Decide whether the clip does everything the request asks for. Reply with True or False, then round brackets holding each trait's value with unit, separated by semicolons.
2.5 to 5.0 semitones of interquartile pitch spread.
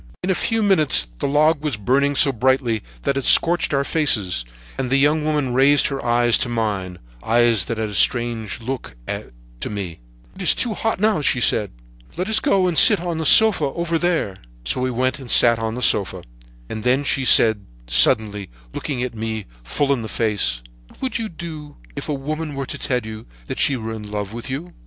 False (5.6 semitones)